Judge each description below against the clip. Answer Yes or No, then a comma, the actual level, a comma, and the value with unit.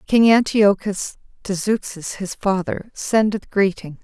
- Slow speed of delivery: Yes, slow, 120 wpm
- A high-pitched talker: Yes, high, 200 Hz